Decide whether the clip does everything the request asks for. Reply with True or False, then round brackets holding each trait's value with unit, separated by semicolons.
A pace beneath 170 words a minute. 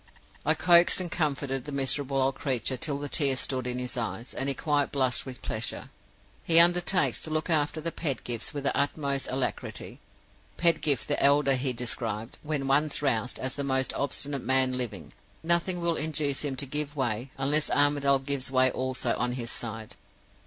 False (180 wpm)